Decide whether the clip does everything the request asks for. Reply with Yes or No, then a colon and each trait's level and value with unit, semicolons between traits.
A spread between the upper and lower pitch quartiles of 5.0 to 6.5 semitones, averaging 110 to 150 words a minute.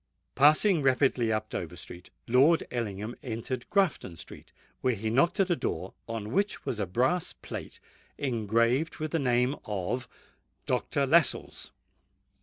Yes: average, 5.3 semitones; average, 140 wpm